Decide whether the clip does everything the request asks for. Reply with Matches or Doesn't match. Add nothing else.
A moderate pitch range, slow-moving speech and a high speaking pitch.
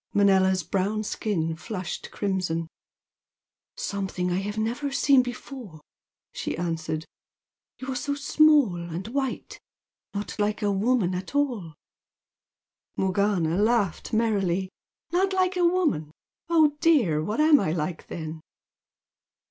Doesn't match